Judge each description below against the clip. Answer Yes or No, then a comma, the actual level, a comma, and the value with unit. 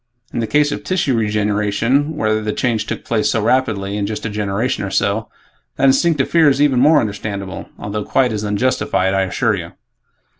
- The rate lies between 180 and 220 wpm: Yes, average, 190 wpm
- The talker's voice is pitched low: Yes, low, 110 Hz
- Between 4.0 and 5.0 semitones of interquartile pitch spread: Yes, average, 4.4 semitones